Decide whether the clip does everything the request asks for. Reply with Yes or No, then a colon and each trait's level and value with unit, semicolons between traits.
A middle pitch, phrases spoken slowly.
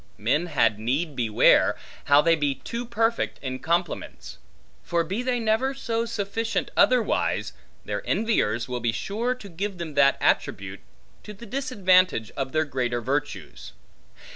No: medium, 170 Hz; average, 145 wpm